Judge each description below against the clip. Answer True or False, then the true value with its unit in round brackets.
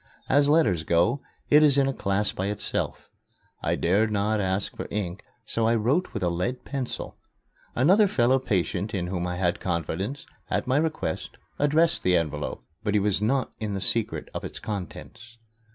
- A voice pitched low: True (105 Hz)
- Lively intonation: True (6.2 semitones)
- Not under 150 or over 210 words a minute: True (180 wpm)